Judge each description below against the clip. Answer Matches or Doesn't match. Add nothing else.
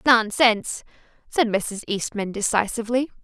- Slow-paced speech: Matches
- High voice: Matches